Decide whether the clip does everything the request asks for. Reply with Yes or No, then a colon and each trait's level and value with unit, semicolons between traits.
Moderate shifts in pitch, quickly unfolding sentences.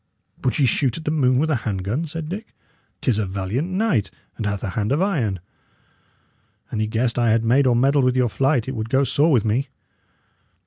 Yes: average, 4.8 semitones; fast, 220 wpm